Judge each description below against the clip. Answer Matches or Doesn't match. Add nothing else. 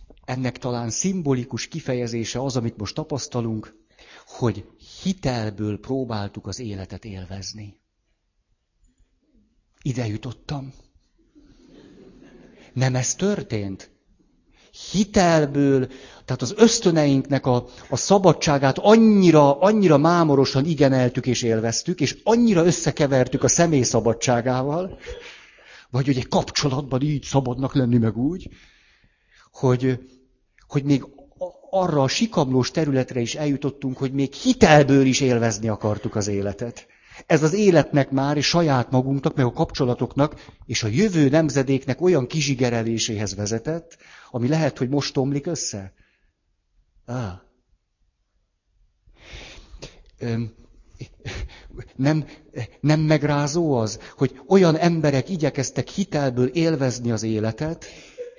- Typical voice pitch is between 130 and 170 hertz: Matches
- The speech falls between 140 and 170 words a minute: Doesn't match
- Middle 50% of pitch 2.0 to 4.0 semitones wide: Doesn't match